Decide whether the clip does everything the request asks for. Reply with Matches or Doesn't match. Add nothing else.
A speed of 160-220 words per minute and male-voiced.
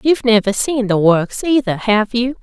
Doesn't match